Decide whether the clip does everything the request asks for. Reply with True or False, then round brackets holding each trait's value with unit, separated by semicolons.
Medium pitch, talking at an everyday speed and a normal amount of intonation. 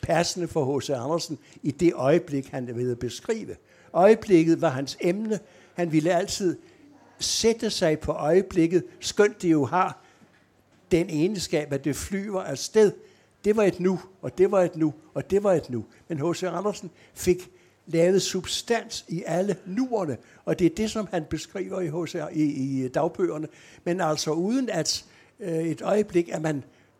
True (170 Hz; 165 wpm; 3.6 semitones)